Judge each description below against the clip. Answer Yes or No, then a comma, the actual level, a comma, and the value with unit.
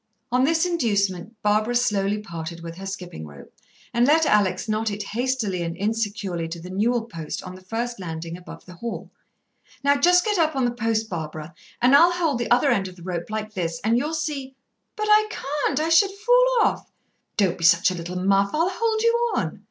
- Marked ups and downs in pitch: Yes, wide, 7.7 semitones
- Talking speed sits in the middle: No, fast, 215 wpm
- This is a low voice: No, high, 215 Hz